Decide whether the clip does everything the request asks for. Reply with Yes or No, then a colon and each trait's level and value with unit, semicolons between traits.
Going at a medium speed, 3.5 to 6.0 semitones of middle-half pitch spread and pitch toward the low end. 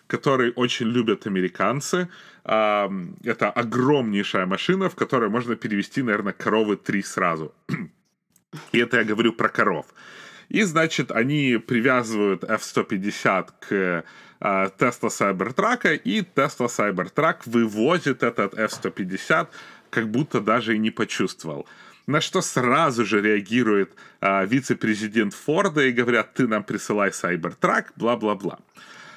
Yes: average, 115 wpm; average, 3.8 semitones; low, 115 Hz